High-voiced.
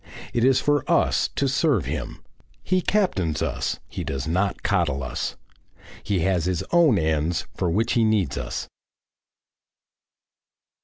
No: very low, 95 Hz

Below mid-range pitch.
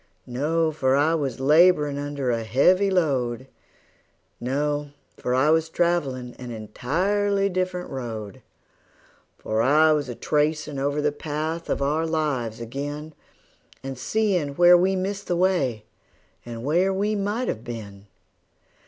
No: medium, 150 Hz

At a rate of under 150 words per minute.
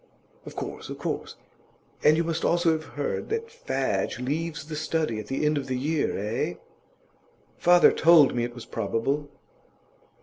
No: average, 165 wpm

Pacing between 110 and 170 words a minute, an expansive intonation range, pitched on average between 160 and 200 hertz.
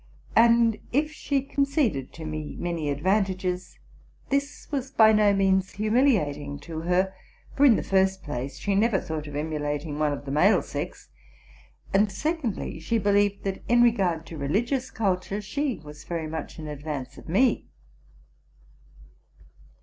Yes: average, 150 wpm; wide, 6.8 semitones; high, 190 Hz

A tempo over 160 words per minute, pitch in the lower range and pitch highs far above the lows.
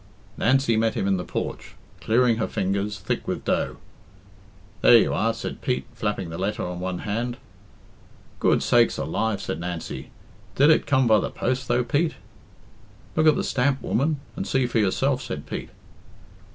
No: average, 170 wpm; low, 115 Hz; average, 4.9 semitones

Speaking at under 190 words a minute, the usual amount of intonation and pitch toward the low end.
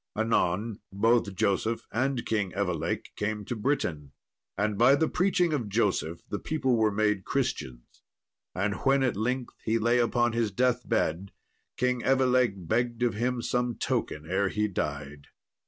Yes: average, 155 wpm; average, 3.7 semitones; low, 110 Hz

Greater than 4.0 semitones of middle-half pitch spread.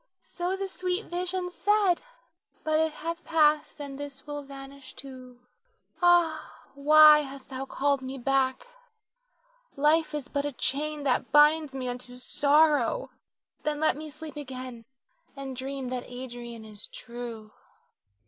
No: average, 3.2 semitones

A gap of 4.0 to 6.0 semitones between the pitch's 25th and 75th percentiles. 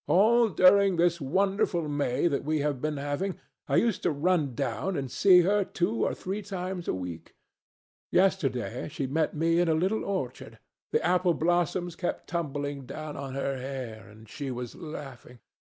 Yes: average, 5.0 semitones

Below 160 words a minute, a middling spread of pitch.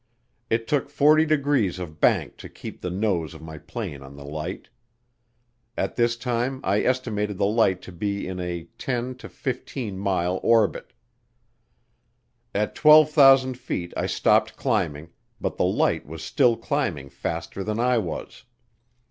No: average, 150 wpm; wide, 6.5 semitones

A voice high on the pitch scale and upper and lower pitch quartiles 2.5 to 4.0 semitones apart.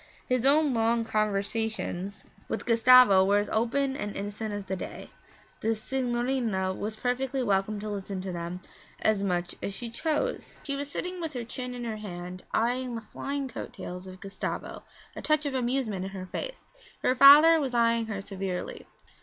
No: high, 225 Hz; average, 4.7 semitones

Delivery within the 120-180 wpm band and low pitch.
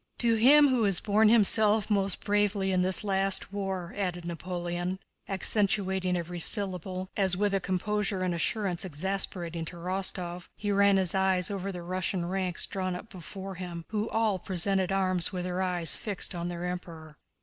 No: average, 170 wpm; high, 190 Hz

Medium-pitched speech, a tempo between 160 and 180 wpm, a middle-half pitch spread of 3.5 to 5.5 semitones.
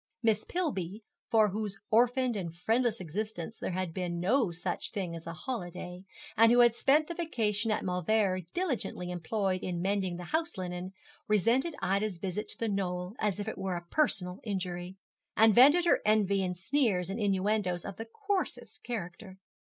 No: high, 200 Hz; average, 175 wpm; average, 4.1 semitones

